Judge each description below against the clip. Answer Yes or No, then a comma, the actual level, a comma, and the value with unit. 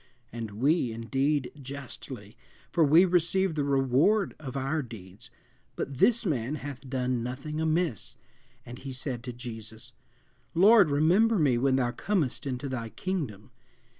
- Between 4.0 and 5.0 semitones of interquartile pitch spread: Yes, average, 4.5 semitones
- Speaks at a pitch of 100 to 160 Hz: Yes, low, 135 Hz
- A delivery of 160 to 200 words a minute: No, average, 140 wpm